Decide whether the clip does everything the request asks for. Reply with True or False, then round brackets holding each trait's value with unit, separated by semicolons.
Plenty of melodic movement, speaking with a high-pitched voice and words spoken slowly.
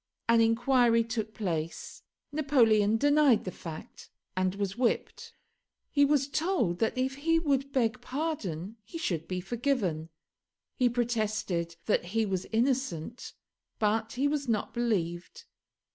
True (5.7 semitones; 230 Hz; 130 wpm)